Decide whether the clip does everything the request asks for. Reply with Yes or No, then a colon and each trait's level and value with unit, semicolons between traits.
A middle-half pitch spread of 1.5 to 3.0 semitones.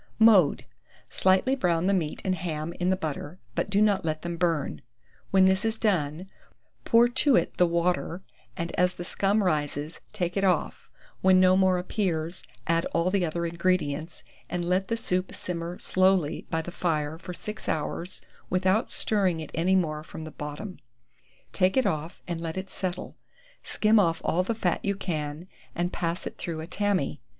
Yes: narrow, 2.6 semitones